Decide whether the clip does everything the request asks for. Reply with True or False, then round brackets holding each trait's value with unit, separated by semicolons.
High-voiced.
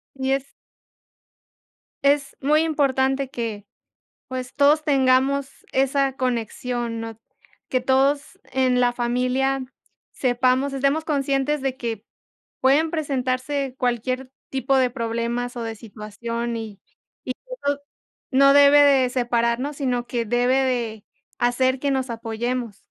True (255 Hz)